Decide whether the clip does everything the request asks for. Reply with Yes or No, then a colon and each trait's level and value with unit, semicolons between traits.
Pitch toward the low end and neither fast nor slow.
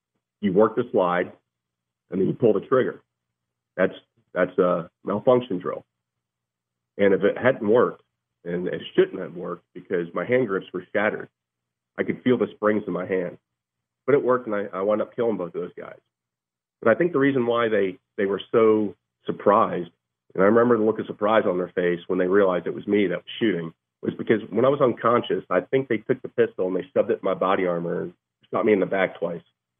No: very low, 90 Hz; fast, 220 wpm